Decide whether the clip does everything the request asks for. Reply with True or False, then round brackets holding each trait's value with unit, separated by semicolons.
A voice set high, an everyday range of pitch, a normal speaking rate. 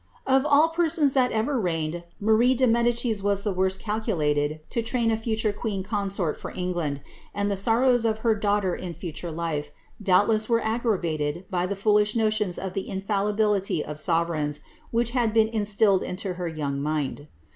True (205 Hz; 4.5 semitones; 175 wpm)